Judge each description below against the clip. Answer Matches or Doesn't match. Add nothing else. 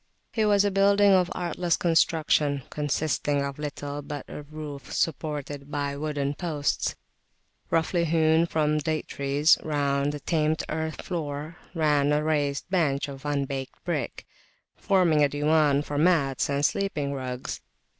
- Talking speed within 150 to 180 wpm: Doesn't match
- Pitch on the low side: Doesn't match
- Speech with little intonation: Matches